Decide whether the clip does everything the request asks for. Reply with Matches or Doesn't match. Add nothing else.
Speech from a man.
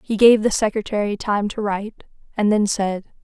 Doesn't match